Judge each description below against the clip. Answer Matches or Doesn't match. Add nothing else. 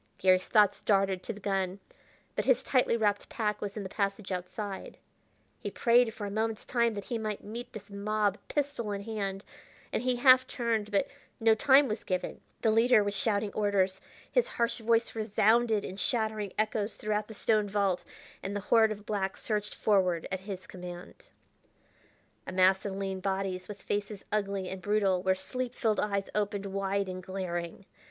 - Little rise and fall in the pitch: Matches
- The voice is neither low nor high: Doesn't match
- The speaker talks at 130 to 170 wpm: Doesn't match